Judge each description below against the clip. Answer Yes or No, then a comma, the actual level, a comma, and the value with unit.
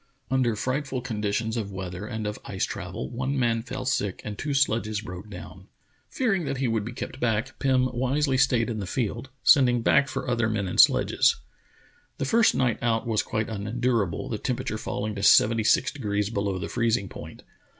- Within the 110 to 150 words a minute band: No, average, 190 wpm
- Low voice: Yes, low, 115 Hz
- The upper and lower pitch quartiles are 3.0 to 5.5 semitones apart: Yes, average, 3.7 semitones